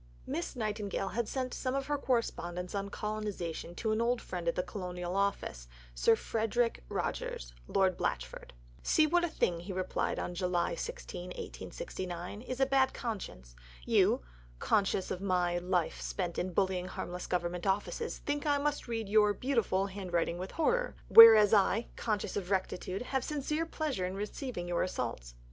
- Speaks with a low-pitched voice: No, high, 200 Hz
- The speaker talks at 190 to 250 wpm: No, average, 160 wpm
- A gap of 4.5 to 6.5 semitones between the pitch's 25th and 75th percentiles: Yes, average, 5.2 semitones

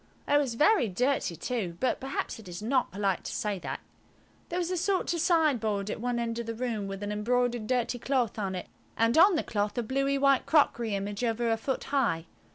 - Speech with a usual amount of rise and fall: Yes, average, 4.7 semitones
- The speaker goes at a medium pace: No, fast, 220 wpm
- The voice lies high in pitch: Yes, high, 235 Hz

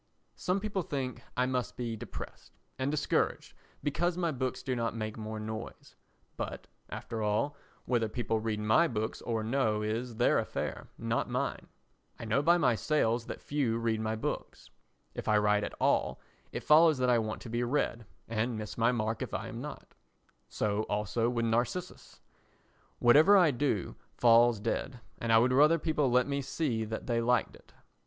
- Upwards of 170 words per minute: Yes, average, 180 wpm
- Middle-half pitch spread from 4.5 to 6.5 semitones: No, average, 3.9 semitones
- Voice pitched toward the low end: Yes, low, 120 Hz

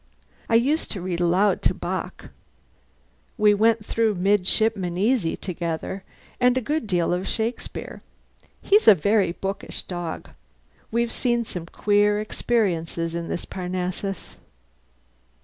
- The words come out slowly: Yes, slow, 125 wpm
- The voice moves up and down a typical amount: Yes, average, 4.1 semitones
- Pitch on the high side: Yes, high, 200 Hz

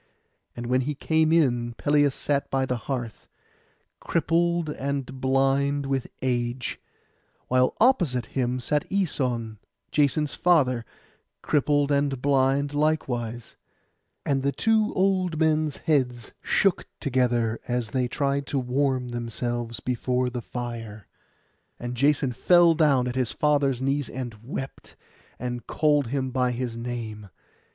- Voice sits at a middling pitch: No, low, 130 Hz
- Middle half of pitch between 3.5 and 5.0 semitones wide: No, average, 3.1 semitones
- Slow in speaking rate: Yes, slow, 130 wpm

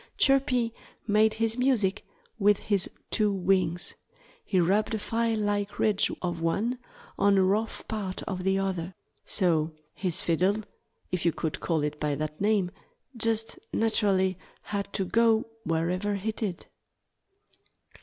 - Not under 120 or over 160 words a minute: Yes, average, 140 wpm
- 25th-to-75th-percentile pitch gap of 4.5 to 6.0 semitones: No, average, 3.5 semitones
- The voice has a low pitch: No, high, 200 Hz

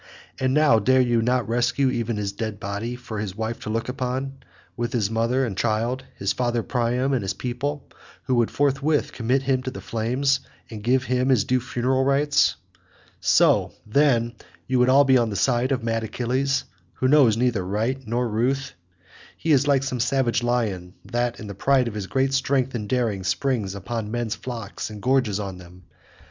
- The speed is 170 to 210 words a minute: Yes, average, 190 wpm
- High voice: No, low, 120 Hz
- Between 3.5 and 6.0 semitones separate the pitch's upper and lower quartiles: No, average, 3.0 semitones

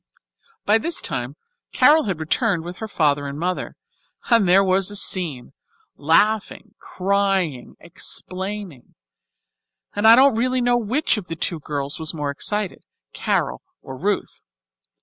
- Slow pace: No, average, 145 wpm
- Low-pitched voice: No, high, 190 Hz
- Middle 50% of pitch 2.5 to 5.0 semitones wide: No, wide, 5.4 semitones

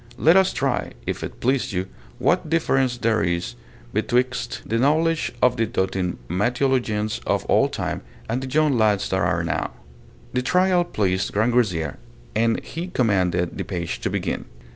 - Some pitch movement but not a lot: No, wide, 5.9 semitones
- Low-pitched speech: Yes, low, 115 Hz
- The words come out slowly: No, average, 160 wpm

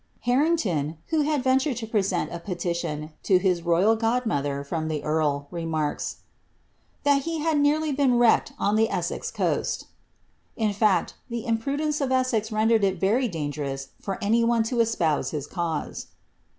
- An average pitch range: No, wide, 7.2 semitones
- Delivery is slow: No, average, 165 wpm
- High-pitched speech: Yes, high, 215 Hz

